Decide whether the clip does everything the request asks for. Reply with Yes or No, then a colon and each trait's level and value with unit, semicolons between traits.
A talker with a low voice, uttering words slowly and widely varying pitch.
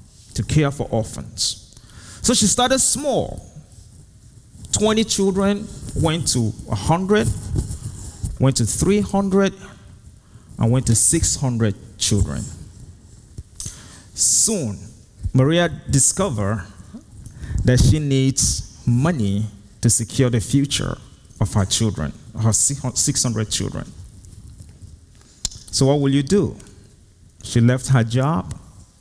No: low, 110 Hz; slow, 95 wpm; average, 4.9 semitones